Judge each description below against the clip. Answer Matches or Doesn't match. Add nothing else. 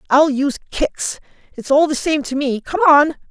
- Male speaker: Doesn't match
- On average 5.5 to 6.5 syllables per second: Doesn't match